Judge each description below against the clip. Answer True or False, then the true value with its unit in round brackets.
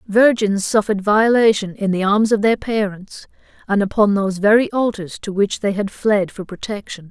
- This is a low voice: False (205 Hz)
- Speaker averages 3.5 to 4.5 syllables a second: False (5.0 syllables/s)